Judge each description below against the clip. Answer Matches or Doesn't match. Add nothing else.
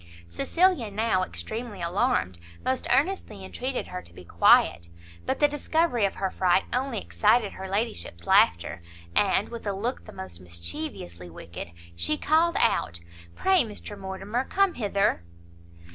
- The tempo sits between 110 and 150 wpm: Matches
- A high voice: Matches